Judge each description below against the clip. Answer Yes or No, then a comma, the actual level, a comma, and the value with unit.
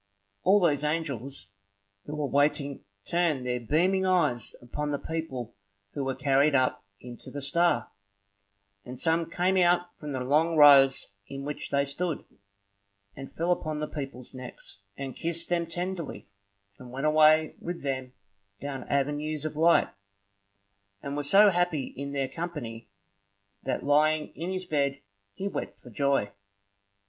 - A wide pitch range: No, average, 3.6 semitones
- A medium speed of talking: Yes, average, 150 wpm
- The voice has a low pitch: No, medium, 145 Hz